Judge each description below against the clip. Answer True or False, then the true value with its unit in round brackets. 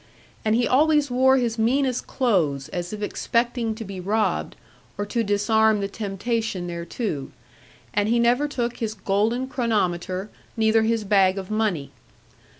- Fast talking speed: False (150 wpm)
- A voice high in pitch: True (220 Hz)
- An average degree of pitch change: True (3.4 semitones)